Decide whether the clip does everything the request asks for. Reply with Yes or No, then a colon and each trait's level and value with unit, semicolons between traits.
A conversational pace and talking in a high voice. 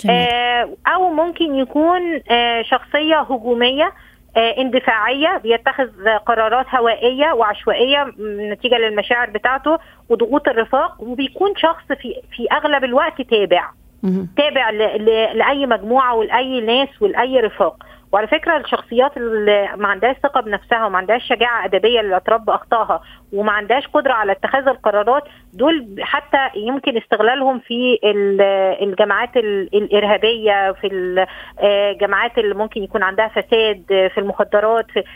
Yes: average, 110 wpm; high, 235 Hz